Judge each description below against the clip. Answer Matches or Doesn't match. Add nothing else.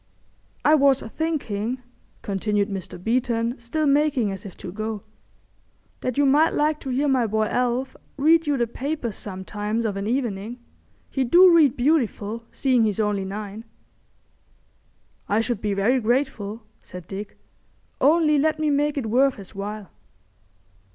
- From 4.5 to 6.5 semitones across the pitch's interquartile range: Matches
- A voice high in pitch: Matches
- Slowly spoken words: Doesn't match